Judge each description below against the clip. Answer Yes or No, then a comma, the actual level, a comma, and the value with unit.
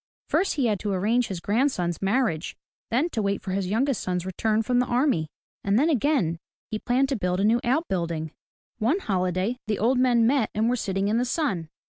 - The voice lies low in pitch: No, high, 220 Hz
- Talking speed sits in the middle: No, fast, 210 wpm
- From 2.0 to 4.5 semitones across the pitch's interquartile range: No, average, 5.0 semitones